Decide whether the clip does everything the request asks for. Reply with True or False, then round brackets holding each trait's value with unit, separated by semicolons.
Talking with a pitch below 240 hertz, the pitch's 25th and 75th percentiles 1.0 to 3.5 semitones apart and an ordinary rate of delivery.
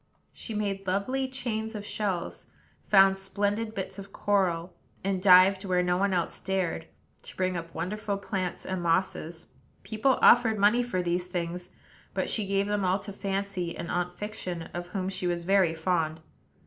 True (190 Hz; 2.4 semitones; 170 wpm)